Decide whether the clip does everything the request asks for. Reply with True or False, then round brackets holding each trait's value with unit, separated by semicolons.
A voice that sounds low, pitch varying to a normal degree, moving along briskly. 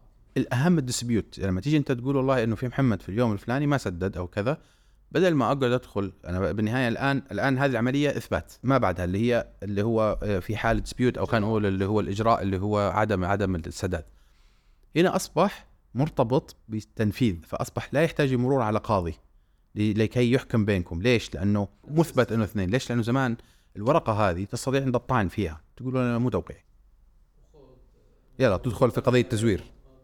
True (115 Hz; 4.7 semitones; 170 wpm)